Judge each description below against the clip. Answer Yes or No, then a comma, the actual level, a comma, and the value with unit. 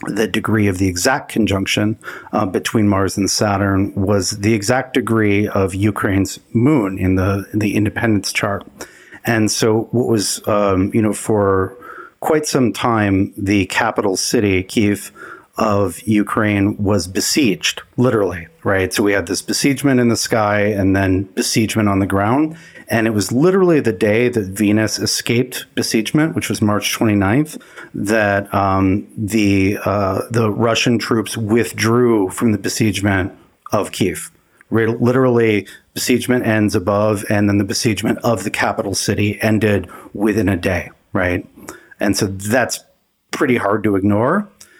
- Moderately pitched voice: No, low, 105 Hz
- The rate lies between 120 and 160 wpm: Yes, average, 150 wpm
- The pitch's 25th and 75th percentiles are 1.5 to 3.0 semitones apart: Yes, narrow, 2.4 semitones